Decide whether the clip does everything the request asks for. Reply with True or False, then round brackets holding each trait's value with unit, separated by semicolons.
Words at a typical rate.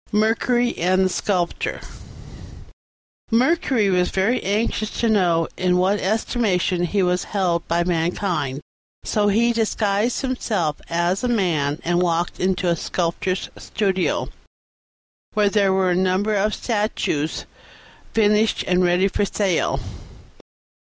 False (125 wpm)